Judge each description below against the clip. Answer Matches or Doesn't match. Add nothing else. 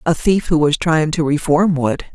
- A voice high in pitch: Doesn't match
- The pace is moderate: Doesn't match